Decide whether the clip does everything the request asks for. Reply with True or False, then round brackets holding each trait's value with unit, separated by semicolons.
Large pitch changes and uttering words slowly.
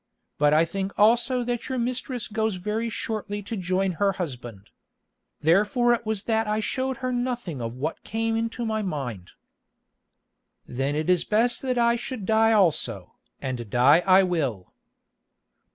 False (6.4 semitones; 155 wpm)